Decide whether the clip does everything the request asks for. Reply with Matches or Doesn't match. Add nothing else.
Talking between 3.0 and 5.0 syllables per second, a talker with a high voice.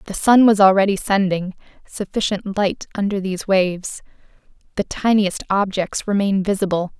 Doesn't match